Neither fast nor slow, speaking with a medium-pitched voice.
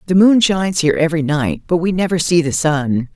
No: fast, 230 wpm; medium, 165 Hz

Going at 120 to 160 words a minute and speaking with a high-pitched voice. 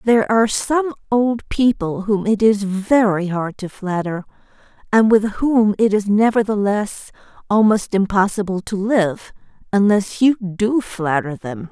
Yes: average, 140 wpm; high, 205 Hz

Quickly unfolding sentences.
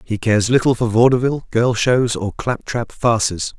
No: average, 185 wpm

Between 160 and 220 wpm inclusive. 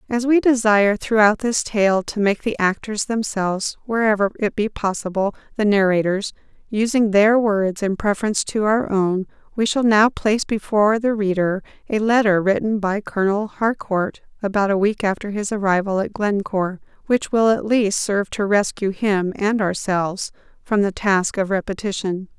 Yes: average, 165 wpm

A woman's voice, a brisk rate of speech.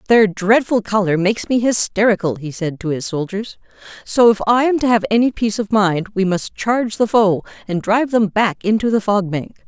Yes: female; fast, 210 wpm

